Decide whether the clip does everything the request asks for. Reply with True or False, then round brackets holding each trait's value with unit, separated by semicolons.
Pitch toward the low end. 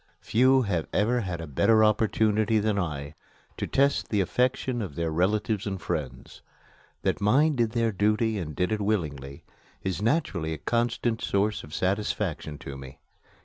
True (105 Hz)